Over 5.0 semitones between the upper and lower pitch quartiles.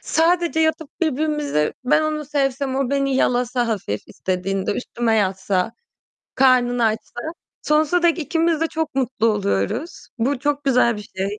Yes: wide, 5.6 semitones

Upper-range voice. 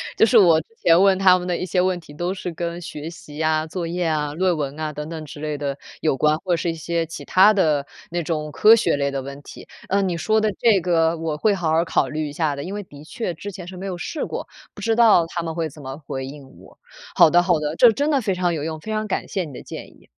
No: medium, 165 Hz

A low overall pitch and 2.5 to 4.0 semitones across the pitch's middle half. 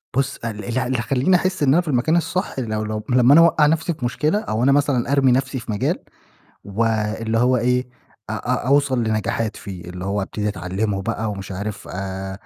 No: low, 120 Hz; average, 4.5 semitones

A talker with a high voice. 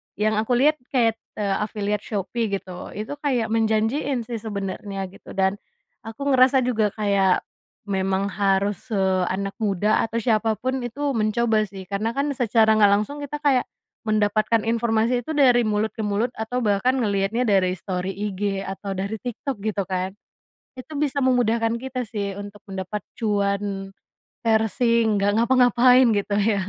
Yes: high, 215 Hz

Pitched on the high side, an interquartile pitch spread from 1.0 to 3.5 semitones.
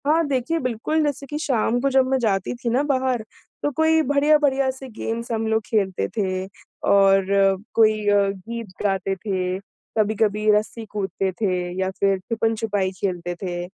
No: high, 220 Hz; average, 5.1 semitones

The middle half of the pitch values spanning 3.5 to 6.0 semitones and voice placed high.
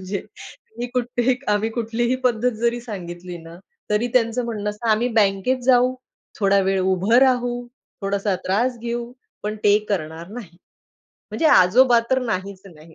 Yes: average, 4.0 semitones; high, 220 Hz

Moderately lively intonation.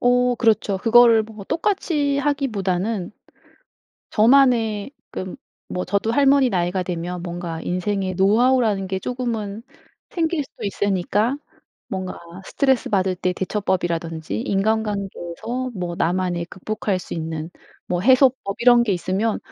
Yes: average, 4.9 semitones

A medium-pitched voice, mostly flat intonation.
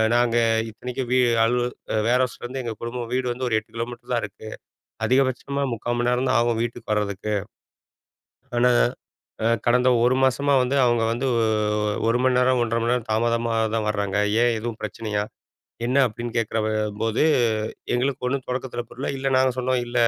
No: low, 120 Hz; narrow, 1.9 semitones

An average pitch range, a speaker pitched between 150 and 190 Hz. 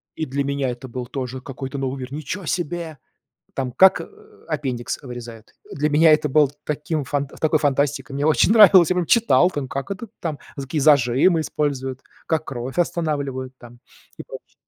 No: average, 3.2 semitones; medium, 140 Hz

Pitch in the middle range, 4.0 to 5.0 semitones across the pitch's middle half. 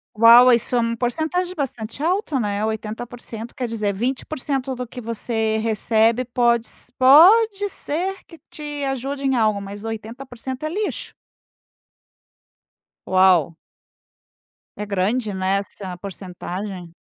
No: high, 235 Hz; average, 4.3 semitones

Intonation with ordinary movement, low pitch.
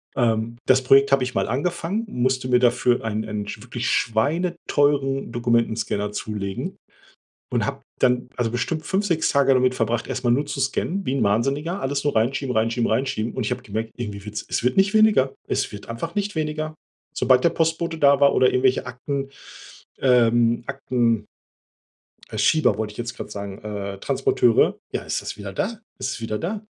Yes: average, 4.0 semitones; low, 125 Hz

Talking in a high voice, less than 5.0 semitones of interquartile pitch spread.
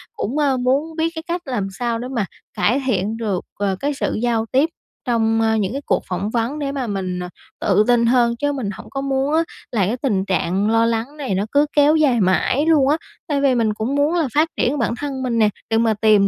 Yes: high, 240 Hz; average, 4.6 semitones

